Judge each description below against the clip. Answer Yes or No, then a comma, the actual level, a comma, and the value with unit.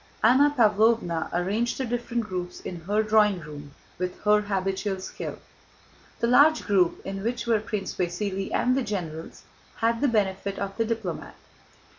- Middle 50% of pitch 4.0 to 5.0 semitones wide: No, average, 3.6 semitones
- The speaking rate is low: No, average, 155 wpm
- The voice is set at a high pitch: Yes, high, 210 Hz